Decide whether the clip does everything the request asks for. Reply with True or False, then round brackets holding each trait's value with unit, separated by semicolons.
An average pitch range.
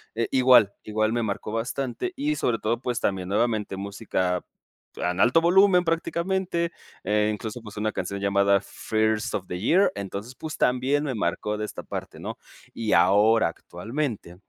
True (4.9 semitones)